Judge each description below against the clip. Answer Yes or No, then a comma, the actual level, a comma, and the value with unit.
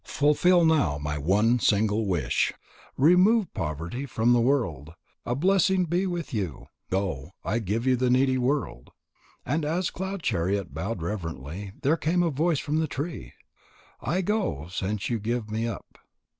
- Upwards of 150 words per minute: Yes, average, 160 wpm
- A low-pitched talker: Yes, low, 120 Hz